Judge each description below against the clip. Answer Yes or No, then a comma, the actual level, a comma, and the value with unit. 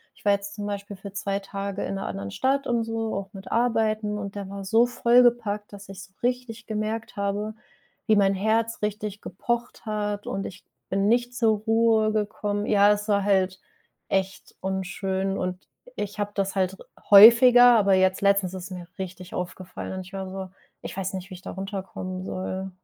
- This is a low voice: No, high, 200 Hz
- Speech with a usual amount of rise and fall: No, narrow, 2.2 semitones